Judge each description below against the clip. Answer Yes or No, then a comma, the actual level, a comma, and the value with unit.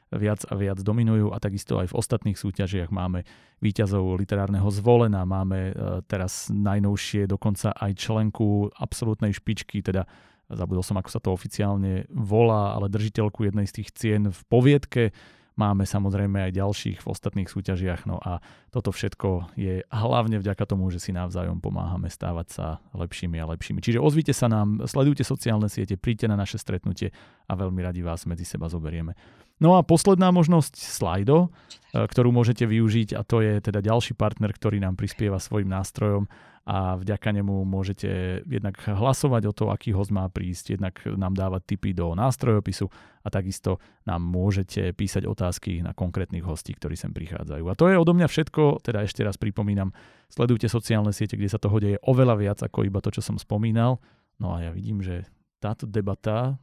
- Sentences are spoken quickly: Yes, fast, 170 wpm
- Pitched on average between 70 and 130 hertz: Yes, low, 100 Hz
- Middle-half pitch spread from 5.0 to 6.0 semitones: No, average, 2.7 semitones